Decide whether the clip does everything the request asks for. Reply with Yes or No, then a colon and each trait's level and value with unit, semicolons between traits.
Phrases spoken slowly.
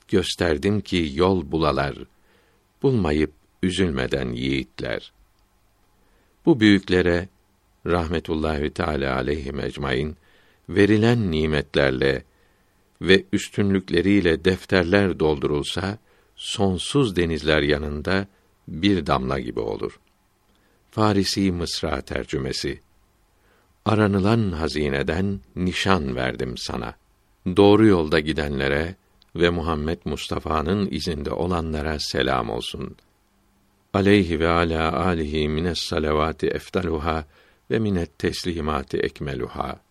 Yes: slow, 85 wpm